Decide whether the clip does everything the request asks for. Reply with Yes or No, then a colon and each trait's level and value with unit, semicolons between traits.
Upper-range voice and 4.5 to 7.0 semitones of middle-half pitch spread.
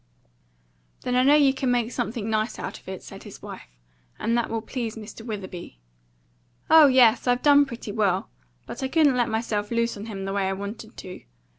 No: high, 230 Hz; average, 3.4 semitones